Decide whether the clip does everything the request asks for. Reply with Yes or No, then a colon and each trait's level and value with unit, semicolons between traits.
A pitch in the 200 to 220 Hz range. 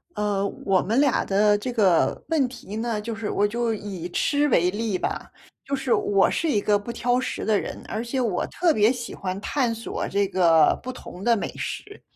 Yes: high, 215 Hz